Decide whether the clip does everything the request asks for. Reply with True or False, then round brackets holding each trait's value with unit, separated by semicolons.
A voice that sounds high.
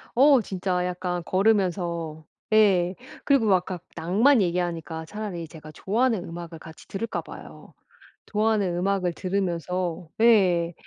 False (180 Hz)